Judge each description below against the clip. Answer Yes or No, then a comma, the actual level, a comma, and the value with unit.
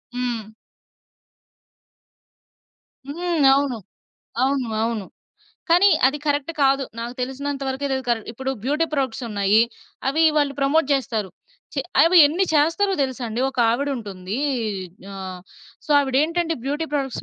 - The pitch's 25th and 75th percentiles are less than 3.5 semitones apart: No, average, 3.8 semitones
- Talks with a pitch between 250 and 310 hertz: Yes, very high, 270 Hz